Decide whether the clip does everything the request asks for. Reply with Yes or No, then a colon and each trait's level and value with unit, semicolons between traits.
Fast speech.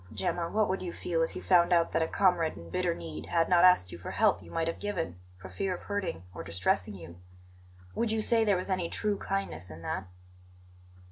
Yes: fast, 225 wpm